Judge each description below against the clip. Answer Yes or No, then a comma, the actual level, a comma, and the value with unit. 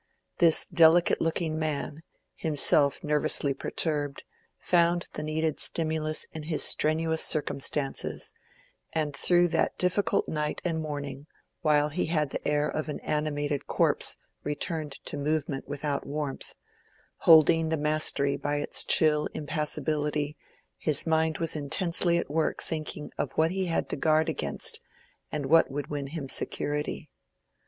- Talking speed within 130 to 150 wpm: Yes, slow, 135 wpm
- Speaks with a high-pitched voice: No, medium, 155 Hz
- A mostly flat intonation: Yes, narrow, 1.6 semitones